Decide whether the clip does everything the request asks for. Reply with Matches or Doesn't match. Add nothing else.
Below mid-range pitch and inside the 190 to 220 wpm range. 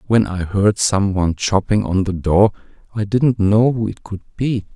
Matches